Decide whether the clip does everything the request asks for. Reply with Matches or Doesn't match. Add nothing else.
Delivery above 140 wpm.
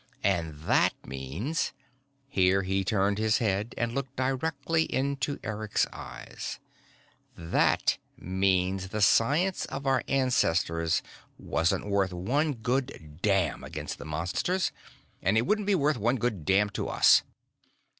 Doesn't match